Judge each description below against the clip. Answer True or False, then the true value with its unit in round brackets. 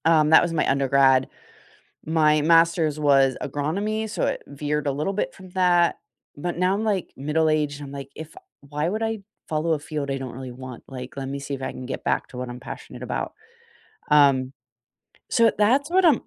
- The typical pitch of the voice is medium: True (150 Hz)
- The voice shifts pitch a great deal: False (4.0 semitones)